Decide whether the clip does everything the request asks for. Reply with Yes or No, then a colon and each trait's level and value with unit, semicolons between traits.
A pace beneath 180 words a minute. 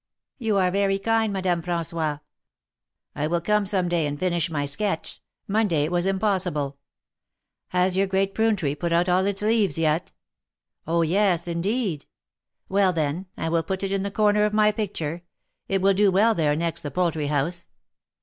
No: average, 185 wpm